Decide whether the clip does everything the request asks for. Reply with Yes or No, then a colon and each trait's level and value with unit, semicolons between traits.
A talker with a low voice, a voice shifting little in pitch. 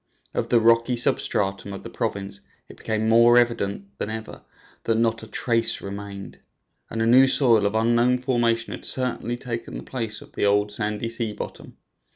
Yes: low, 115 Hz; narrow, 2.2 semitones